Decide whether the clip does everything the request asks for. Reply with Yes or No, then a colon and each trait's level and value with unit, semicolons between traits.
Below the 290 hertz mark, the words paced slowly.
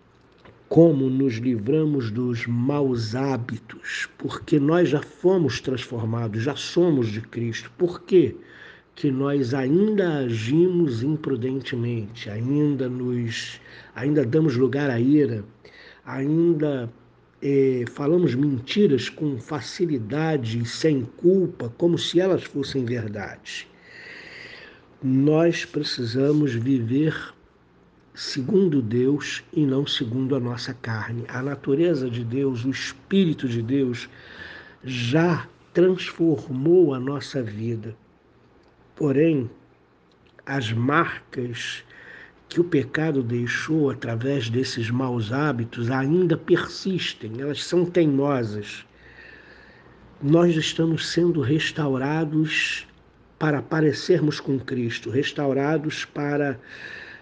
Yes: medium, 140 Hz; slow, 100 wpm